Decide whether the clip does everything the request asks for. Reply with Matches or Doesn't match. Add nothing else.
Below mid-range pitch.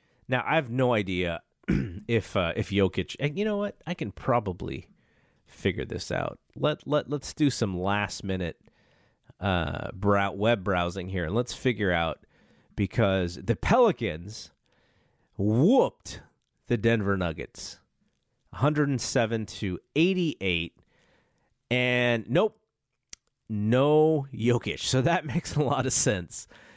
Matches